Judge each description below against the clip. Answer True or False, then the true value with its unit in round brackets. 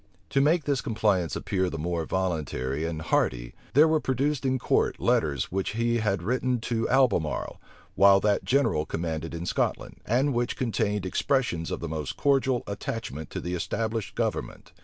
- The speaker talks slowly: False (165 wpm)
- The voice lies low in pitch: True (105 Hz)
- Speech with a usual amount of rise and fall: False (7.5 semitones)